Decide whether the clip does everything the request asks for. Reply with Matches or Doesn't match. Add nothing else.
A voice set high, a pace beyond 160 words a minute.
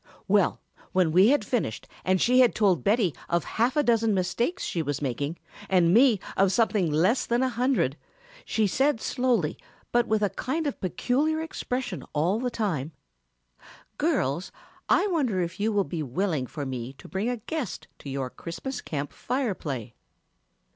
Matches